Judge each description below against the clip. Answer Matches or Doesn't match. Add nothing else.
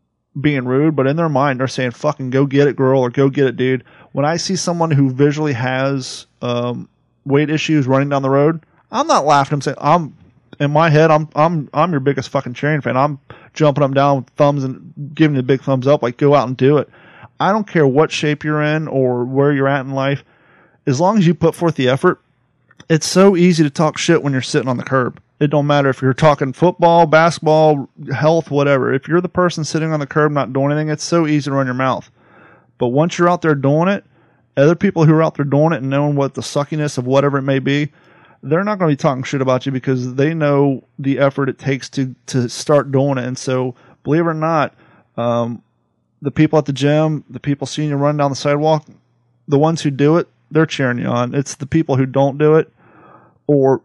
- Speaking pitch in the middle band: Matches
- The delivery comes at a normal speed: Doesn't match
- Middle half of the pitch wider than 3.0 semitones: Doesn't match